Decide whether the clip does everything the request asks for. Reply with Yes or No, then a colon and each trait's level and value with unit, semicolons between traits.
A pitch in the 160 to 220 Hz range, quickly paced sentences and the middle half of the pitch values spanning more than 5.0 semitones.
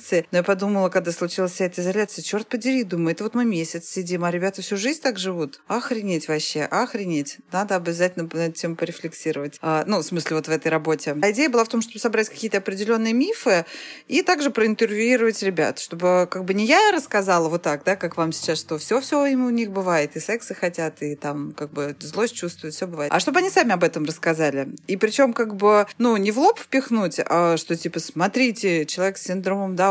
Yes: medium, 185 Hz; fast, 210 wpm; wide, 5.4 semitones